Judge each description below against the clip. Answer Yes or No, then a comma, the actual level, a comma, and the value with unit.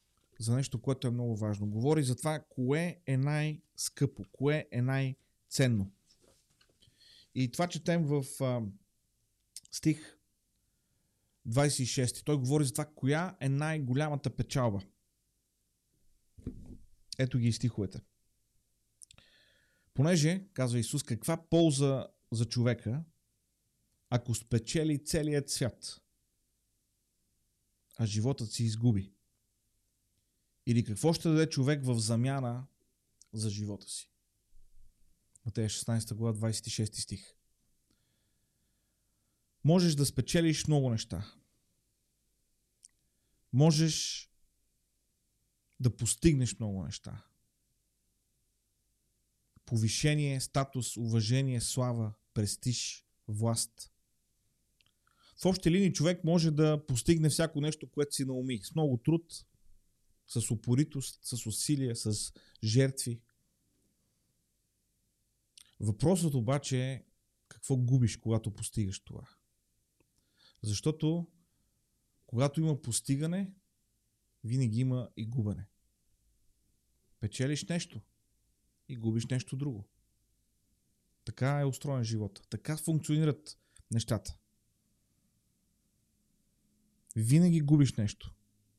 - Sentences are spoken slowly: Yes, slow, 90 wpm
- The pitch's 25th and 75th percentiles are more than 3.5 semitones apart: Yes, average, 4.5 semitones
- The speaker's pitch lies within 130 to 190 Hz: No, low, 120 Hz